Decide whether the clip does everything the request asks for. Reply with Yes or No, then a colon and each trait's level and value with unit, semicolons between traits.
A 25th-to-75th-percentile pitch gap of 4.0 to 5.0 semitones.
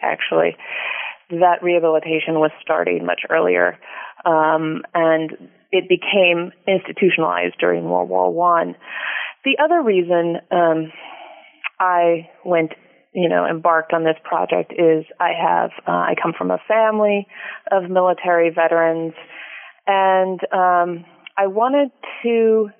No: average, 2.9 semitones